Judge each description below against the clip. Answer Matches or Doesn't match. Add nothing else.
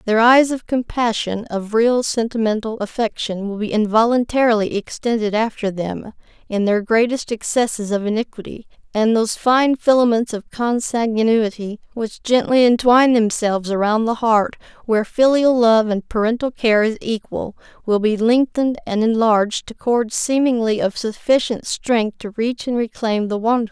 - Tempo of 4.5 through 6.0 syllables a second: Matches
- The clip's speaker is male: Doesn't match